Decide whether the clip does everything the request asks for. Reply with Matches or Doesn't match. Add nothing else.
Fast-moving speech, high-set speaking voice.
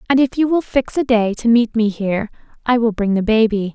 Matches